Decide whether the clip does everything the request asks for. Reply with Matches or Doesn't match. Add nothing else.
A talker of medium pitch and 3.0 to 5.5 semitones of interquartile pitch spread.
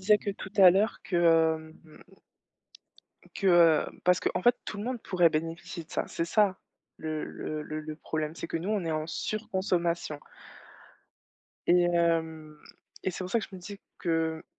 Matches